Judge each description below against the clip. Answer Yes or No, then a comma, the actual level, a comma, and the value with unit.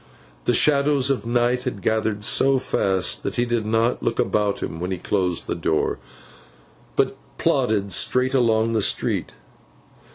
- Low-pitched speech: Yes, low, 115 Hz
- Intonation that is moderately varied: Yes, average, 3.7 semitones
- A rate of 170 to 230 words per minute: No, average, 155 wpm